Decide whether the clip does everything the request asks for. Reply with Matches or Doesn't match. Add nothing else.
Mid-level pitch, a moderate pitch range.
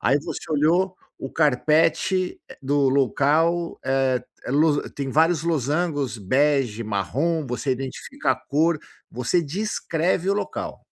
Matches